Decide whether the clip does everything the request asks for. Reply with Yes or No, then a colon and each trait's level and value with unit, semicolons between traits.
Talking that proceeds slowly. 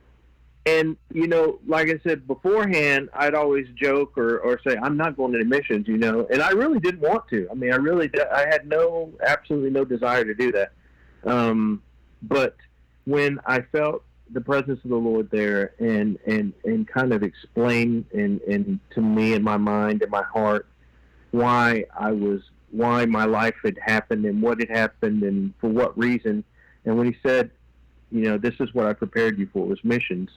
No: average, 195 wpm